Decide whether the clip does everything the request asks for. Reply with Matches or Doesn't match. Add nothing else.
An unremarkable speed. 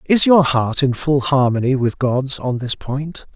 Matches